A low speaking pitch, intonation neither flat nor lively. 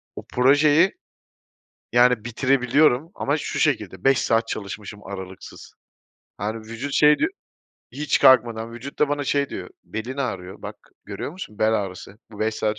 Yes: low, 120 Hz; average, 4.7 semitones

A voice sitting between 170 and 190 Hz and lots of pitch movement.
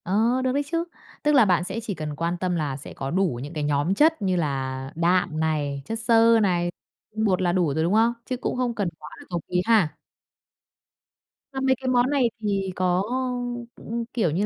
Yes: medium, 185 Hz; wide, 6.3 semitones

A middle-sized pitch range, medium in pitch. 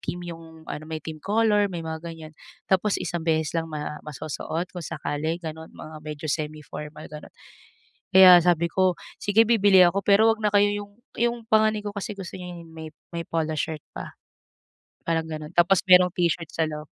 Yes: average, 3.9 semitones; medium, 170 Hz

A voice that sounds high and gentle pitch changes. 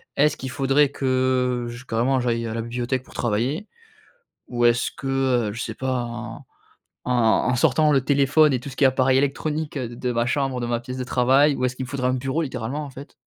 No: low, 130 Hz; narrow, 2.2 semitones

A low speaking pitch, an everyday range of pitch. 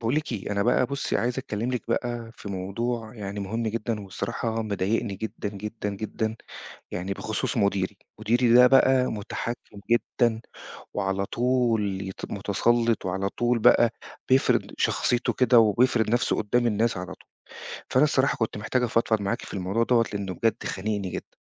Yes: low, 110 Hz; average, 3.0 semitones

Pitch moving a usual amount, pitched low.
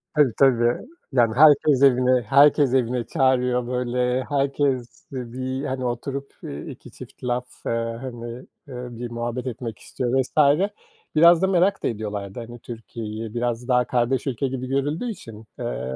No: narrow, 2.2 semitones; low, 125 Hz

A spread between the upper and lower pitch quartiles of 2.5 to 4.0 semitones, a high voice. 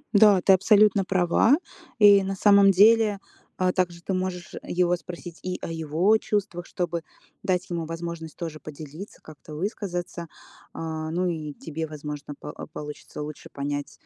No: average, 3.4 semitones; medium, 175 Hz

